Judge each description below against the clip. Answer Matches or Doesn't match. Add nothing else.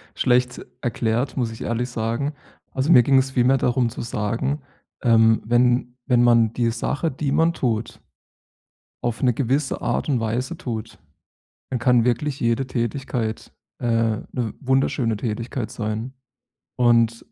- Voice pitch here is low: Matches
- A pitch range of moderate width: Doesn't match